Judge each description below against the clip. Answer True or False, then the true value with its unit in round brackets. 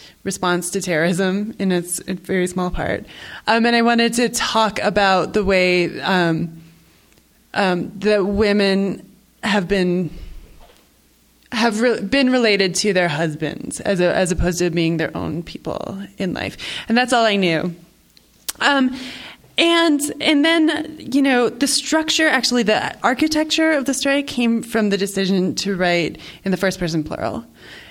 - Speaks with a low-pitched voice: False (200 Hz)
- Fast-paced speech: False (155 wpm)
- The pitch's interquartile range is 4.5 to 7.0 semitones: True (5.4 semitones)